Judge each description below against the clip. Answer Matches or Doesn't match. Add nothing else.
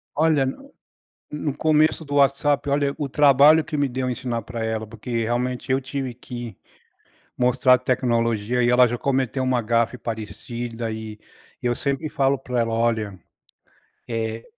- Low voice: Matches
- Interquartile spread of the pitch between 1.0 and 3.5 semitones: Matches